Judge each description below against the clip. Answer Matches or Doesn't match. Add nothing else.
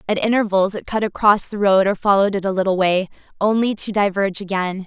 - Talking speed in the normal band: Doesn't match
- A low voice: Doesn't match